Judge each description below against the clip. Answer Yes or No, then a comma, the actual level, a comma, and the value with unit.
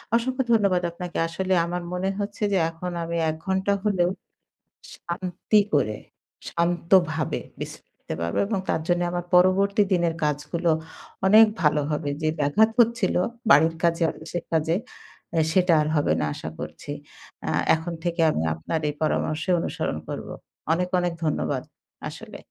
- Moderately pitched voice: Yes, medium, 175 Hz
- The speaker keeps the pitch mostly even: No, average, 3.0 semitones